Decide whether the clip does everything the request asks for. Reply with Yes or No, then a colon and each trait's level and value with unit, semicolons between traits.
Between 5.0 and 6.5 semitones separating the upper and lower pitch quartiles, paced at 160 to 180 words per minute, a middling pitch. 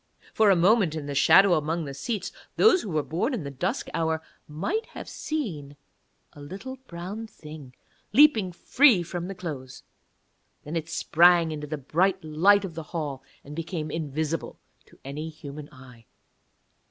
No: average, 4.6 semitones; average, 165 wpm; medium, 165 Hz